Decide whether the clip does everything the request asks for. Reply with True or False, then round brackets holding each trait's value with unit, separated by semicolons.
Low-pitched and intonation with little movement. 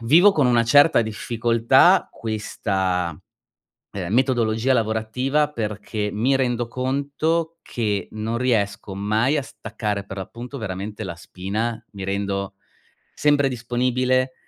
False (115 Hz; 3.8 semitones)